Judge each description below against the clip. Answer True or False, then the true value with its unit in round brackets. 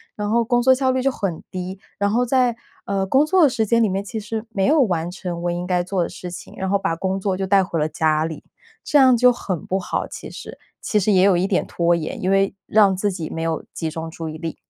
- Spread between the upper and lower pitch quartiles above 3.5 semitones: True (4.2 semitones)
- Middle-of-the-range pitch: False (195 Hz)